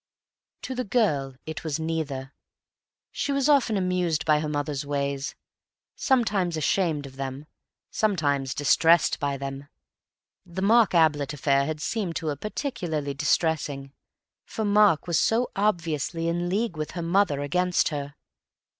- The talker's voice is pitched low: No, medium, 160 Hz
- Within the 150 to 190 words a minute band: No, average, 140 wpm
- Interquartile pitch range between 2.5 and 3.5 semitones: No, average, 5.0 semitones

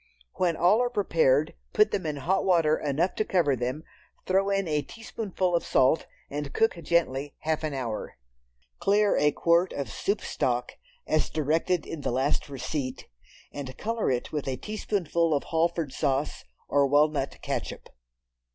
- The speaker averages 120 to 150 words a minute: No, average, 160 wpm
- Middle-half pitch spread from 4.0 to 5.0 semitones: Yes, average, 4.7 semitones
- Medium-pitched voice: Yes, medium, 155 Hz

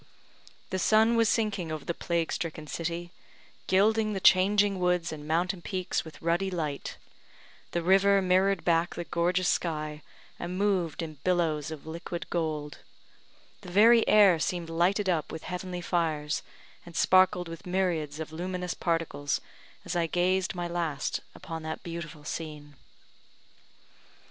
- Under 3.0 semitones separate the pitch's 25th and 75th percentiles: Yes, narrow, 2.6 semitones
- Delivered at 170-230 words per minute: No, average, 145 wpm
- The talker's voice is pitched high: No, medium, 175 Hz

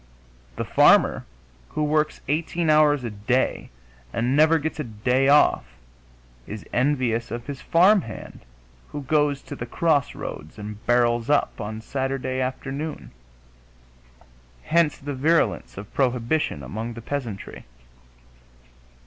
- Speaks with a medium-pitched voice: No, low, 130 Hz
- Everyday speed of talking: No, slow, 120 wpm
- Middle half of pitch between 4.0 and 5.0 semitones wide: Yes, average, 4.3 semitones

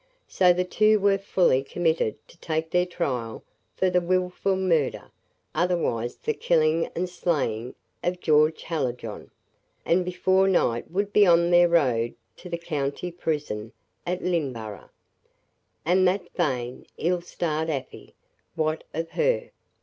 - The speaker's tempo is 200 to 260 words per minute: No, slow, 135 wpm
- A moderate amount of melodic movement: Yes, average, 4.2 semitones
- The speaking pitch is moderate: Yes, medium, 170 Hz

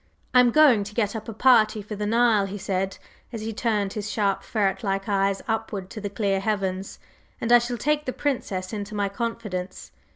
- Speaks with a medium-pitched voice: No, high, 210 Hz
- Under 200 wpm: No, fast, 205 wpm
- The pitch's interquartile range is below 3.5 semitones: Yes, average, 2.8 semitones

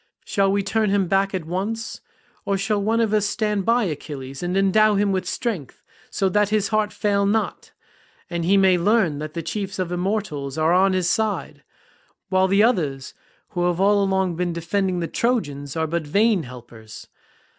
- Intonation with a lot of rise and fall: No, average, 3.5 semitones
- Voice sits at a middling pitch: No, high, 195 Hz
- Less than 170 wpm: No, average, 190 wpm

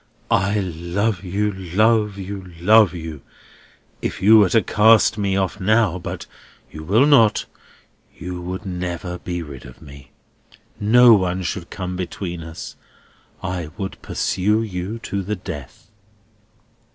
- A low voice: Yes, very low, 95 Hz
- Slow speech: Yes, slow, 130 wpm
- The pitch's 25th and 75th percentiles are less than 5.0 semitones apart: Yes, average, 3.1 semitones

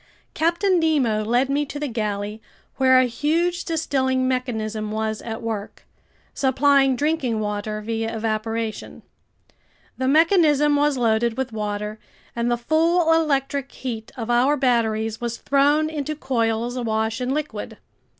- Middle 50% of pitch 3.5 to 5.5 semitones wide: Yes, average, 4.6 semitones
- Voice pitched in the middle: No, very high, 250 Hz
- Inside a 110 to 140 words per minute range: Yes, slow, 135 wpm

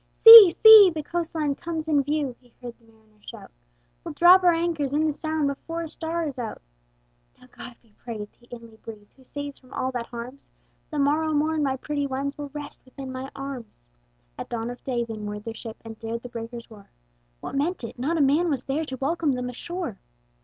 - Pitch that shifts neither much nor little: Yes, average, 4.8 semitones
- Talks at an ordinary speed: No, fast, 215 wpm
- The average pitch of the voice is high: Yes, very high, 275 Hz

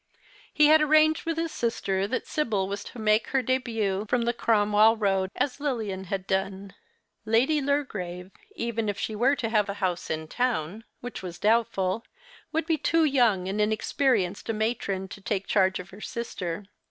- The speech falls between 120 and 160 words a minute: No, average, 175 wpm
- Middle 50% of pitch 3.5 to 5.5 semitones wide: Yes, average, 4.5 semitones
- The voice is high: Yes, high, 215 Hz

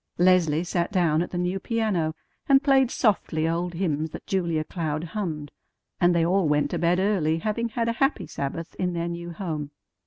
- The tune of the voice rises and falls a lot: No, average, 3.4 semitones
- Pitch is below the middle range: No, medium, 175 Hz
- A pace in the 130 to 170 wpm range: No, average, 190 wpm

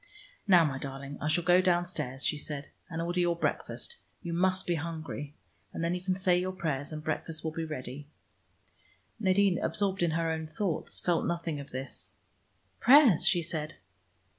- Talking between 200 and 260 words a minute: No, average, 175 wpm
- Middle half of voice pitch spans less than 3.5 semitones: Yes, average, 2.9 semitones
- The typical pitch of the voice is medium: Yes, medium, 165 Hz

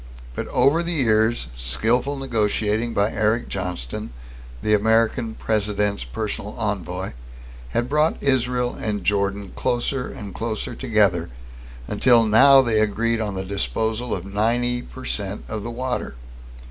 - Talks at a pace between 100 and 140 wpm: Yes, slow, 135 wpm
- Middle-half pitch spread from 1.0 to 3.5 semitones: Yes, average, 3.1 semitones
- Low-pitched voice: Yes, low, 110 Hz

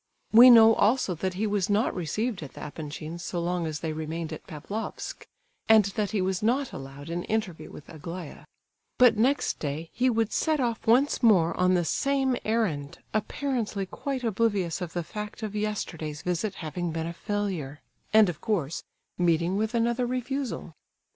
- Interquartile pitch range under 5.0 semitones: No, average, 5.3 semitones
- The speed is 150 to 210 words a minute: Yes, average, 165 wpm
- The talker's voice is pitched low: No, high, 195 Hz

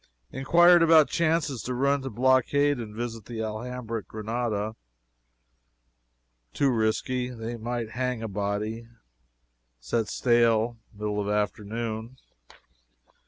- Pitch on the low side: Yes, low, 115 Hz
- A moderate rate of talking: No, slow, 115 wpm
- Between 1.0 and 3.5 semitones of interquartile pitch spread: Yes, average, 2.9 semitones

